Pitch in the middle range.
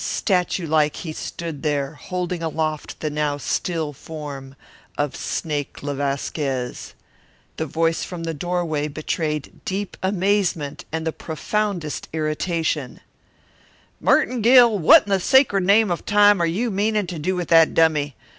Yes: medium, 165 Hz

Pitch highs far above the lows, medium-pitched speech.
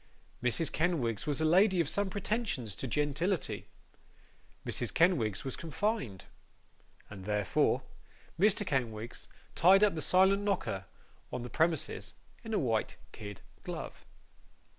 Yes: wide, 8.5 semitones; medium, 155 Hz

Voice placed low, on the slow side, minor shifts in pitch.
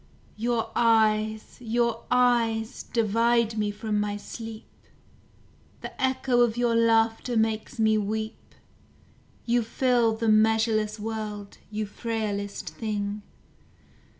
No: high, 225 Hz; slow, 105 wpm; narrow, 1.5 semitones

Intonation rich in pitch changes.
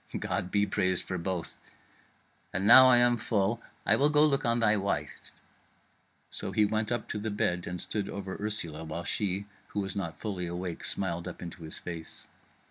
No: average, 3.6 semitones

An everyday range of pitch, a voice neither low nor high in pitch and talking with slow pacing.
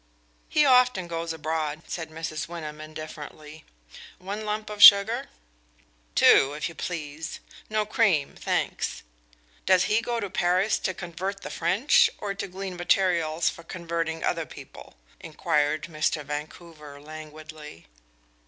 Yes: average, 3.9 semitones; medium, 165 Hz; slow, 130 wpm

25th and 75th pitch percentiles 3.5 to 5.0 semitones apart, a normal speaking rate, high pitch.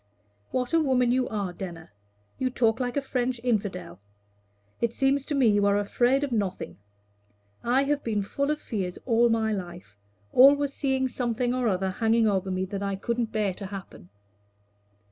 Yes: average, 4.6 semitones; average, 175 wpm; high, 230 Hz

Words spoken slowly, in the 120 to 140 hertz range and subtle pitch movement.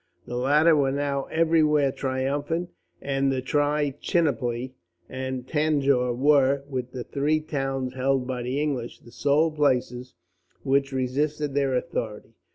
Yes: slow, 125 wpm; low, 135 Hz; narrow, 2.3 semitones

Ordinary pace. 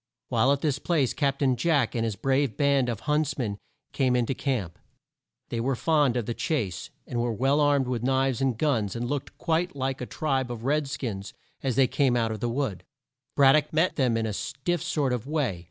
No: fast, 220 wpm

